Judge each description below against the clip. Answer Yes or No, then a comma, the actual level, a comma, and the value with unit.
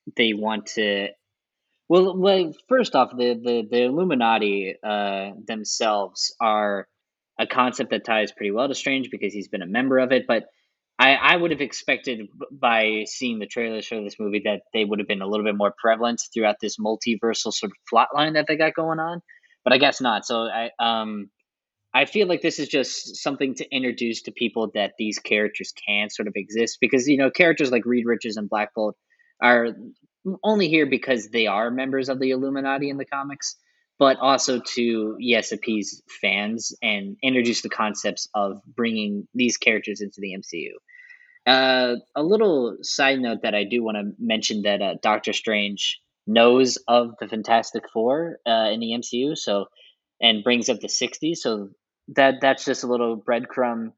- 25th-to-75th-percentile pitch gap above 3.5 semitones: Yes, average, 4.2 semitones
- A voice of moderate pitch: No, low, 120 Hz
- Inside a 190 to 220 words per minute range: No, average, 180 wpm